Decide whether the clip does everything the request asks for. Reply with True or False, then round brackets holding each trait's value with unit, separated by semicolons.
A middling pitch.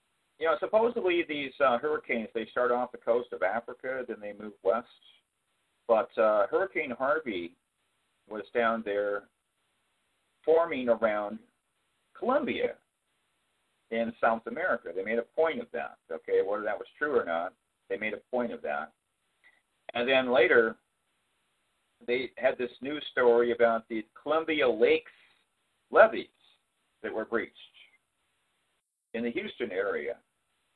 False (125 Hz)